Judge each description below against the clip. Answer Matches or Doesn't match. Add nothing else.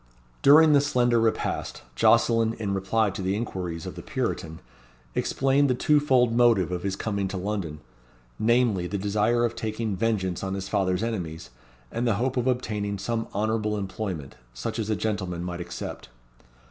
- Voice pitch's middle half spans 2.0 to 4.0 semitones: Matches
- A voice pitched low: Matches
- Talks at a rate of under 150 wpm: Doesn't match